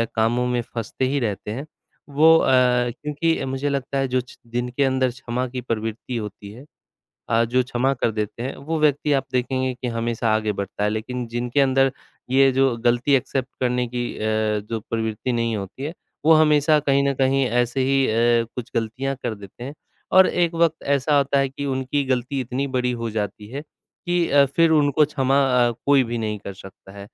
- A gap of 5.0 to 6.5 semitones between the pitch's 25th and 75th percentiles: No, average, 3.0 semitones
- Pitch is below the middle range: Yes, low, 130 Hz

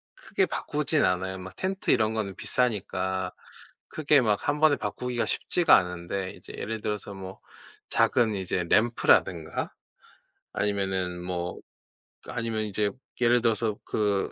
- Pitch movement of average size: Yes, average, 4.1 semitones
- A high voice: No, low, 105 Hz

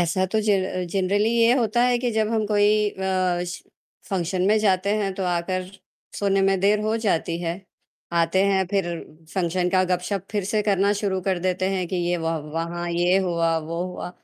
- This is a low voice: No, high, 190 Hz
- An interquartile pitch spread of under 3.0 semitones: Yes, narrow, 2.6 semitones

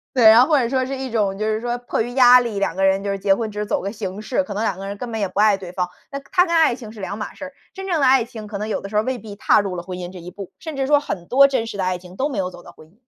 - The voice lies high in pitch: Yes, high, 215 Hz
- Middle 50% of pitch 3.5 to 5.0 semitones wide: Yes, average, 4.6 semitones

